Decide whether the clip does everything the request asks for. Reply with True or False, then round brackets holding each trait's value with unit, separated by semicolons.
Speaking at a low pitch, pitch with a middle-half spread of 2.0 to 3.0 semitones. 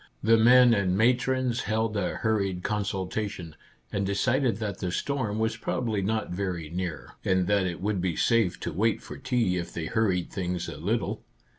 False (105 Hz; 3.7 semitones)